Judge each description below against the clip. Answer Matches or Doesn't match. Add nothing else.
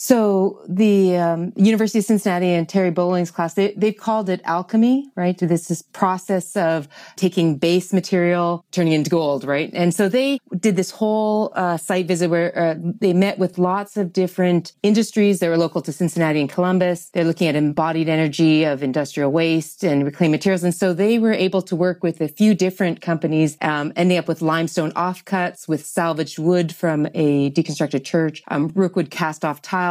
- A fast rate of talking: Doesn't match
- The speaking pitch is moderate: Matches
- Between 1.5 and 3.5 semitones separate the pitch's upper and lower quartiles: Matches